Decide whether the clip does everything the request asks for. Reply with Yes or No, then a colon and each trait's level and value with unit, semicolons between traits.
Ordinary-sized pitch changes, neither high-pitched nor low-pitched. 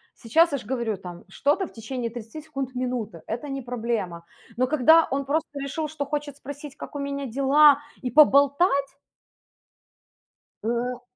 No: average, 3.3 semitones; very high, 275 Hz